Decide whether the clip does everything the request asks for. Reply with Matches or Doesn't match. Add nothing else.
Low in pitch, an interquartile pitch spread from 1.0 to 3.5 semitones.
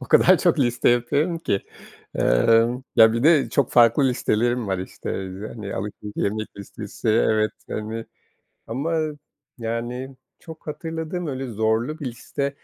Doesn't match